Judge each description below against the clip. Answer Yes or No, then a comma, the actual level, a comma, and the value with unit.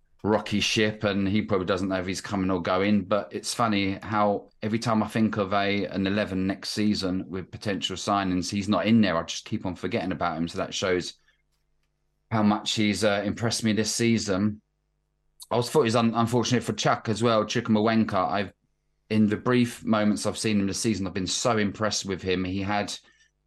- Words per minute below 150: No, fast, 205 wpm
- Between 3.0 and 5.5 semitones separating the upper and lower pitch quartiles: No, narrow, 2.4 semitones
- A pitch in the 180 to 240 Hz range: No, low, 105 Hz